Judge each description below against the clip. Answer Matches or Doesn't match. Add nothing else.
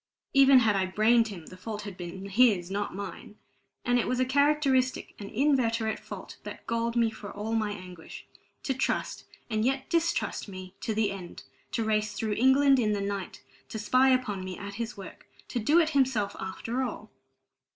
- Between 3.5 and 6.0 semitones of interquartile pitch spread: Matches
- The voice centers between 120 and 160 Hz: Doesn't match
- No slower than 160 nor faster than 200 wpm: Matches